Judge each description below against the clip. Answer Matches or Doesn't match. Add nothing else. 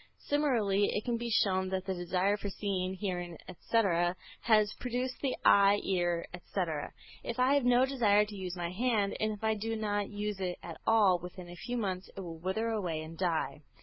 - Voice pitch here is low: Doesn't match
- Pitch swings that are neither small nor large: Matches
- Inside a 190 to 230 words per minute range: Matches